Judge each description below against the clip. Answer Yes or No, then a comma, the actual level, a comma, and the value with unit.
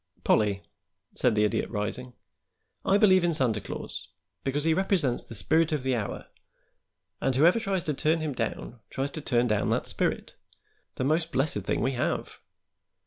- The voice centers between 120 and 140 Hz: Yes, low, 135 Hz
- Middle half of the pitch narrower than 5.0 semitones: No, average, 5.3 semitones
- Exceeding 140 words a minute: Yes, average, 170 wpm